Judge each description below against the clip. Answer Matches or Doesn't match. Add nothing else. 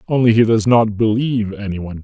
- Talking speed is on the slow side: Doesn't match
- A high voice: Doesn't match